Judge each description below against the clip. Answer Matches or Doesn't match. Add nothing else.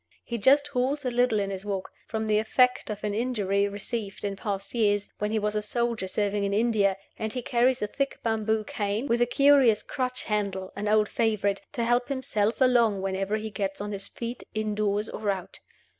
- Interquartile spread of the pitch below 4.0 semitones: Matches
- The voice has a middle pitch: Doesn't match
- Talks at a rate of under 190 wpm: Doesn't match